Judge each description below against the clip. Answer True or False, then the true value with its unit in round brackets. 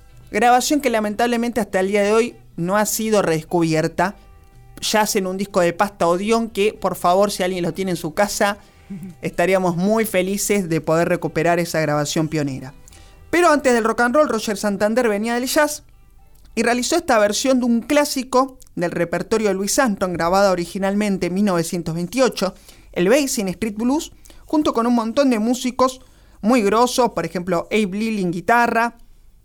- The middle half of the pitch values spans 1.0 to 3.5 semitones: False (5.3 semitones)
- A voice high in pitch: True (205 Hz)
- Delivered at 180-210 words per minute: False (170 wpm)